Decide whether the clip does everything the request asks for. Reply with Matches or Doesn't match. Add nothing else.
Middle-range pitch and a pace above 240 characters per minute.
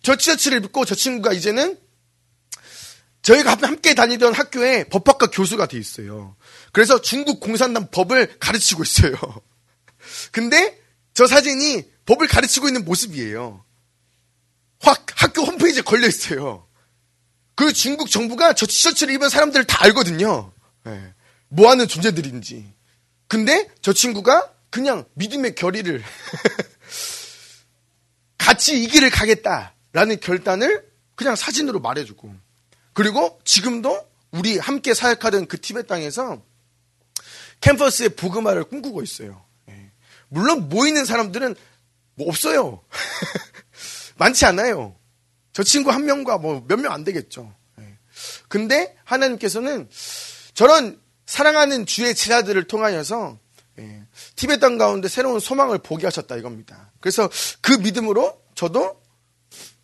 Doesn't match